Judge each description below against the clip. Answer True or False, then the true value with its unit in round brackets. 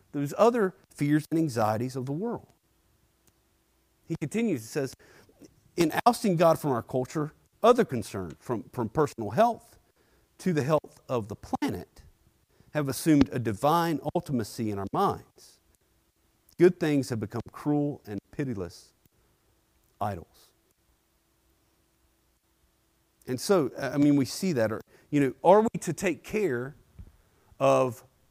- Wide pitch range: True (6.2 semitones)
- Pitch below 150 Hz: True (135 Hz)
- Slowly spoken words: True (130 wpm)